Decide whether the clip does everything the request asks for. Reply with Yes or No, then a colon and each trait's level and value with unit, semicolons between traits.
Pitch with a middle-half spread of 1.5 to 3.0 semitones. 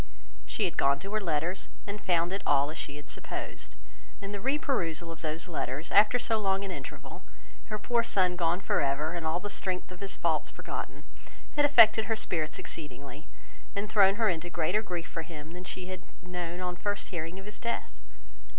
No: average, 3.8 semitones